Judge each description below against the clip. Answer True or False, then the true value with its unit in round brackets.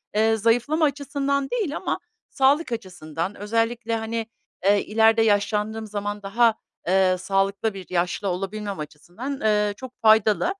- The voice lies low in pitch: False (220 Hz)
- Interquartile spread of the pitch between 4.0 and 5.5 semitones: False (3.1 semitones)